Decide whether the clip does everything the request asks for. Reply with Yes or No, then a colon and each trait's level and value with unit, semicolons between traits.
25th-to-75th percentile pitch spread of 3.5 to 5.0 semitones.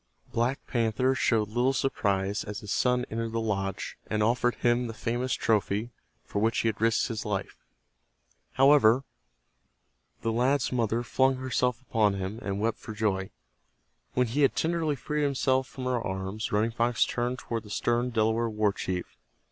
No: average, 2.9 semitones